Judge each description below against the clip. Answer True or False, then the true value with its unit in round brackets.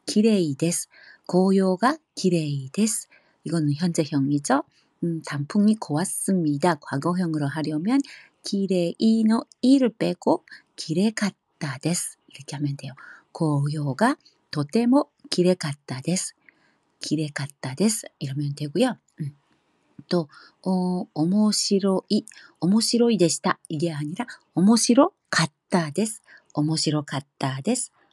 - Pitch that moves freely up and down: True (5.9 semitones)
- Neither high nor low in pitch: True (175 Hz)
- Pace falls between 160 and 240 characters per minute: True (230 characters per minute)